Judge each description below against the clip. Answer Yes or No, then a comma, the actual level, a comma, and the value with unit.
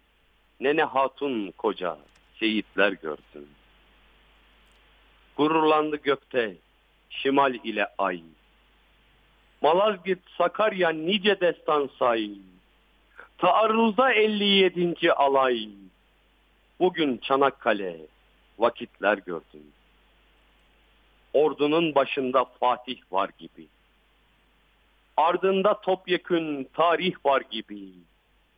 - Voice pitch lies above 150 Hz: No, medium, 140 Hz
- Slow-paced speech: Yes, slow, 65 wpm